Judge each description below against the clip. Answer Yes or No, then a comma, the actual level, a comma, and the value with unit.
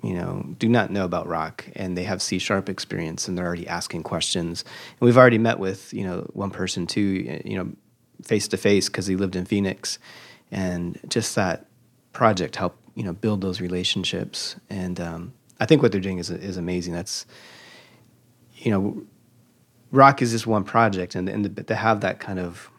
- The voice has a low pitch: Yes, very low, 95 Hz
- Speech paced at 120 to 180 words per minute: No, average, 190 wpm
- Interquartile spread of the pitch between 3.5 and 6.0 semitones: Yes, average, 3.8 semitones